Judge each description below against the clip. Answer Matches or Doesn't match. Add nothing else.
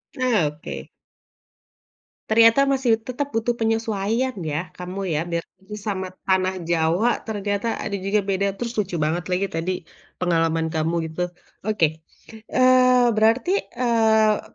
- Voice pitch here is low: Doesn't match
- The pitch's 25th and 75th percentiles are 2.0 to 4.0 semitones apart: Doesn't match